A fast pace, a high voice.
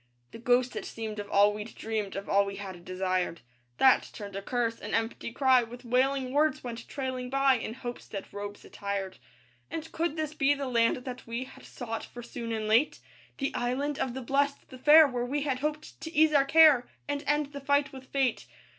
Yes: fast, 210 wpm; very high, 250 Hz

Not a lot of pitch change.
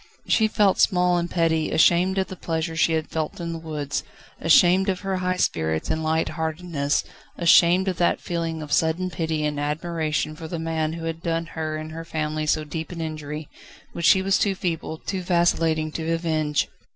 Yes: narrow, 1.9 semitones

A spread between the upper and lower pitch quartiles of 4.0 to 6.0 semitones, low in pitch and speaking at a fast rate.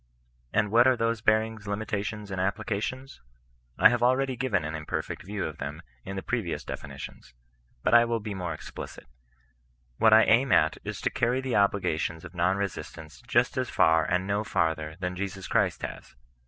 No: average, 4.5 semitones; low, 100 Hz; average, 175 wpm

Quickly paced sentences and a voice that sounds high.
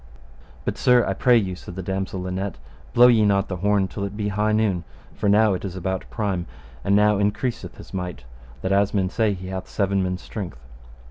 No: fast, 210 wpm; low, 100 Hz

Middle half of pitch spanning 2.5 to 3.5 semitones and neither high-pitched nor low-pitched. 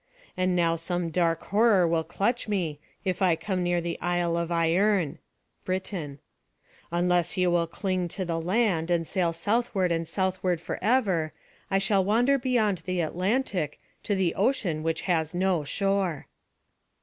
Yes: average, 2.8 semitones; medium, 180 Hz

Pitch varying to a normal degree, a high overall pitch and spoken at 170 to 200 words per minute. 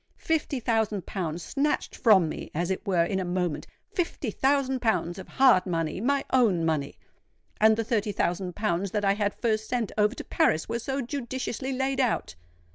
No: wide, 5.9 semitones; high, 215 Hz; average, 175 wpm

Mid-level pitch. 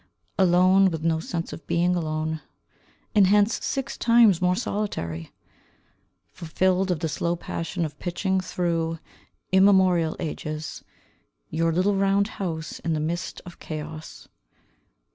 Yes: medium, 175 Hz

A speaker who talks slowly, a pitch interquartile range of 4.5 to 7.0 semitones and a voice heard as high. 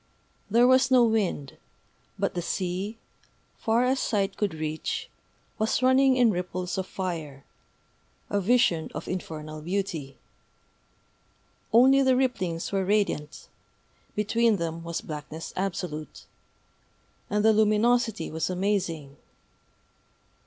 Yes: slow, 110 wpm; wide, 5.5 semitones; high, 195 Hz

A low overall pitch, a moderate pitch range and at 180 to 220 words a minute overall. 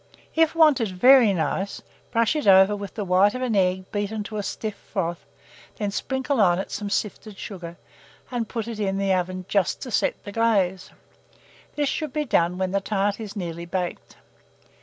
No: high, 200 Hz; average, 3.4 semitones; average, 185 wpm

